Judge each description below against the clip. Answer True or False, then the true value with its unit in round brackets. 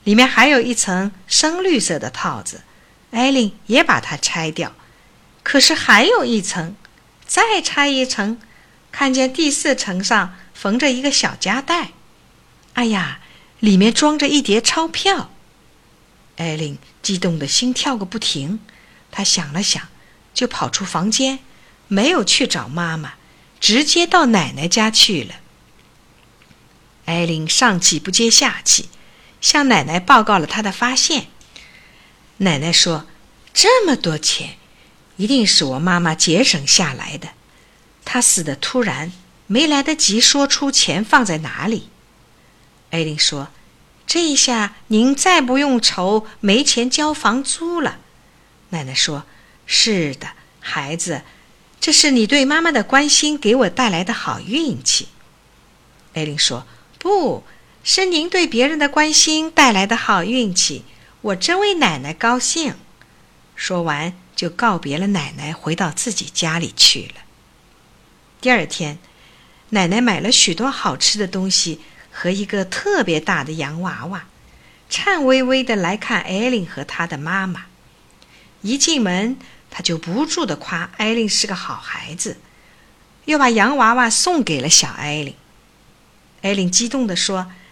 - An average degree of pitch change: False (7.5 semitones)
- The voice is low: False (215 Hz)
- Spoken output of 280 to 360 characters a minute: False (200 characters per minute)